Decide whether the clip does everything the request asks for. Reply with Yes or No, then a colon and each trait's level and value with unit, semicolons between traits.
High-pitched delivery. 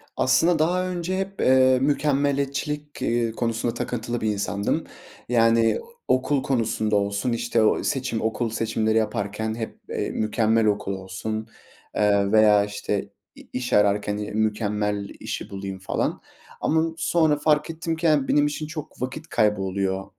No: low, 115 Hz